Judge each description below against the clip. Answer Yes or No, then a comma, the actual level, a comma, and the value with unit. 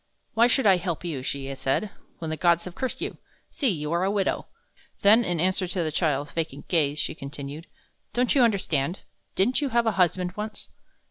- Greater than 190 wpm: Yes, average, 200 wpm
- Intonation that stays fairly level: No, wide, 5.5 semitones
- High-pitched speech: No, medium, 175 Hz